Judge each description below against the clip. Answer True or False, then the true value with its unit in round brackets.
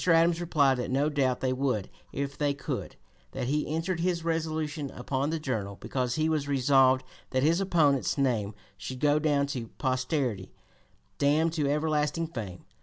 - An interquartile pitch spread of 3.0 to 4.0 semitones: True (3.4 semitones)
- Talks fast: False (165 wpm)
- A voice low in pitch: False (145 Hz)